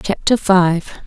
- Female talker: Yes, female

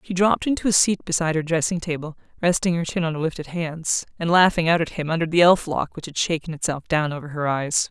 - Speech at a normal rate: No, fast, 250 wpm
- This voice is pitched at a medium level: Yes, medium, 165 Hz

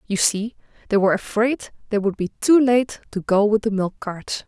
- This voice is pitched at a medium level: No, high, 215 Hz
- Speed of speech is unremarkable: No, fast, 215 wpm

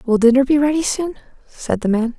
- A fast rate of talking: Yes, fast, 220 wpm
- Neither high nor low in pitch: No, very high, 260 Hz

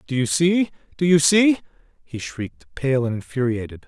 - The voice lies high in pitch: No, medium, 150 Hz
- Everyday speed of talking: Yes, average, 170 wpm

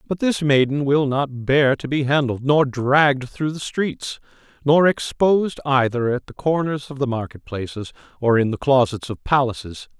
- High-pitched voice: No, low, 135 Hz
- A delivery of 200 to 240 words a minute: No, average, 180 wpm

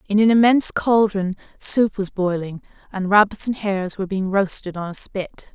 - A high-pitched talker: Yes, high, 195 Hz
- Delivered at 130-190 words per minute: Yes, average, 185 wpm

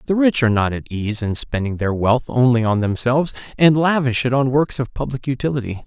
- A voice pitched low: Yes, low, 125 Hz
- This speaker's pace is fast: Yes, fast, 215 wpm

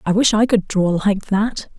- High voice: Yes, high, 205 Hz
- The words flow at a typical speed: No, fast, 235 wpm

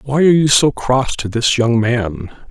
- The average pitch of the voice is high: No, low, 125 Hz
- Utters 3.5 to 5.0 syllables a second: Yes, 4.4 syllables/s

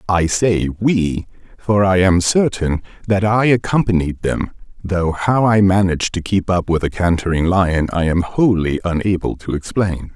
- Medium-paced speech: Yes, average, 165 wpm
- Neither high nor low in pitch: No, very low, 95 Hz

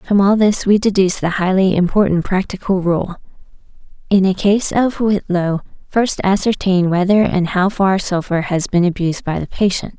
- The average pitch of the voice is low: No, high, 190 Hz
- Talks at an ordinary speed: Yes, average, 170 wpm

